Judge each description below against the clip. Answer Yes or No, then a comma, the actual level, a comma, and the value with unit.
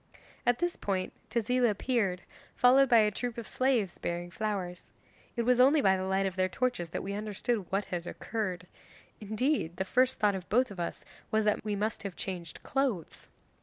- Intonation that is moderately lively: Yes, average, 4.7 semitones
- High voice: Yes, high, 210 Hz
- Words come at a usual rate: Yes, average, 190 wpm